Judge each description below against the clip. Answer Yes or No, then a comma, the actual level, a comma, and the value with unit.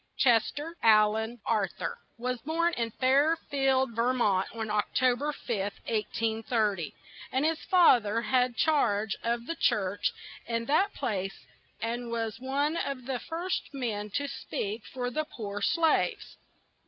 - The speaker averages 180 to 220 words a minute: No, average, 155 wpm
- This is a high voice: Yes, high, 240 Hz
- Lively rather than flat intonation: No, average, 4.3 semitones